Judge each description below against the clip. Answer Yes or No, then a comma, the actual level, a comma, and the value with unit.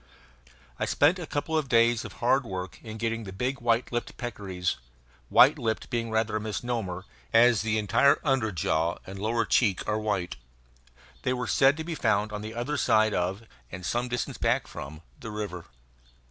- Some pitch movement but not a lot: Yes, average, 3.4 semitones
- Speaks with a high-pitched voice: No, low, 110 Hz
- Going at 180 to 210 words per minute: Yes, average, 185 wpm